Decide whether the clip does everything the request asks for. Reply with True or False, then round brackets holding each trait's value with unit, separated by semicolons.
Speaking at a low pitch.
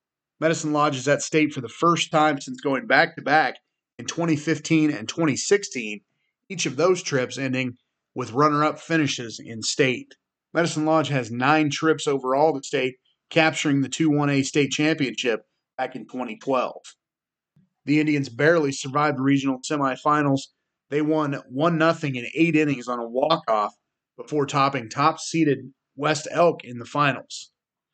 False (145 Hz)